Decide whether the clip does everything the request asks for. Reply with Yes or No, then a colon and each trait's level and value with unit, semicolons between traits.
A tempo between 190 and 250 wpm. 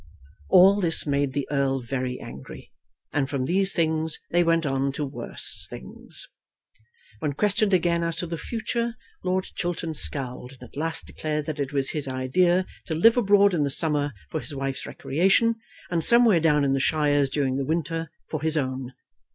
No: average, 180 wpm